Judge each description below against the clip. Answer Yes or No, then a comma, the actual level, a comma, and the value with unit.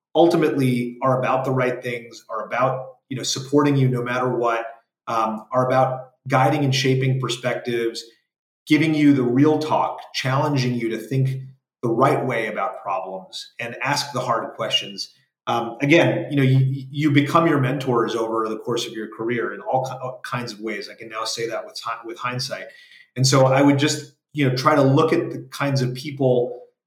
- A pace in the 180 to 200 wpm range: Yes, average, 190 wpm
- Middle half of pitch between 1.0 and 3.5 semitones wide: Yes, average, 2.8 semitones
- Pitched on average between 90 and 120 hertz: No, low, 130 Hz